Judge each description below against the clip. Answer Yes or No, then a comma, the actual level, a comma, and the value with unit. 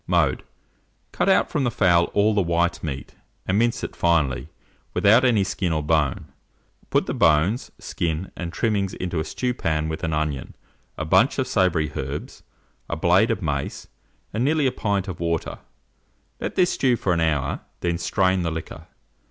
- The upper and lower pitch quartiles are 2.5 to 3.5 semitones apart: No, average, 4.5 semitones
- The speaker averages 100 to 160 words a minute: No, average, 175 wpm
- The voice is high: No, very low, 85 Hz